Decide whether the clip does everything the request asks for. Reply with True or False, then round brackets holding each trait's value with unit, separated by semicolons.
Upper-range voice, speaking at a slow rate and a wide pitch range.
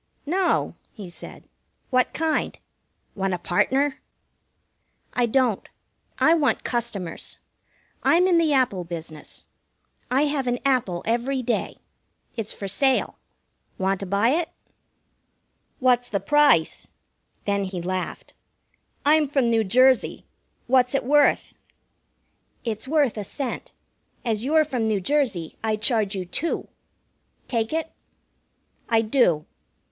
True (245 Hz; 120 wpm; 5.9 semitones)